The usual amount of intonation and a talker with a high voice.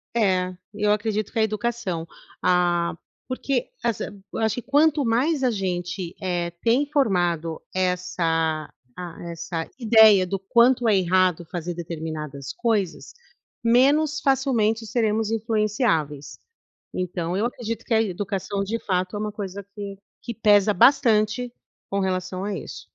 Yes: average, 4.3 semitones; high, 205 Hz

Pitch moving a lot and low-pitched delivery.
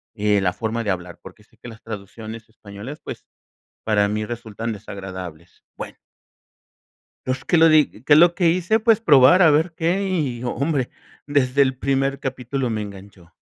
Yes: wide, 6.1 semitones; low, 120 Hz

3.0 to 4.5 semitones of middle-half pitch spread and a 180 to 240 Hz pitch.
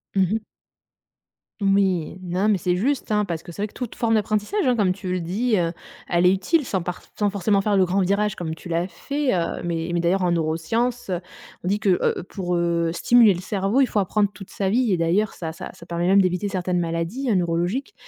Yes: average, 3.4 semitones; high, 190 Hz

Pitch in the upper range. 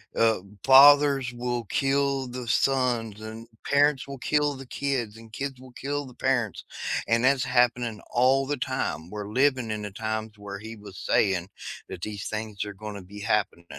No: low, 120 Hz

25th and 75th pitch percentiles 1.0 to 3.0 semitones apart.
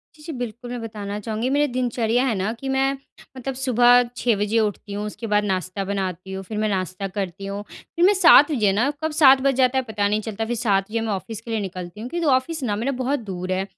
No: average, 4.3 semitones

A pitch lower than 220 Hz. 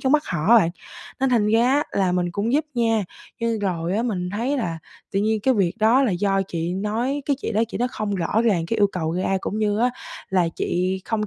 Yes: high, 210 Hz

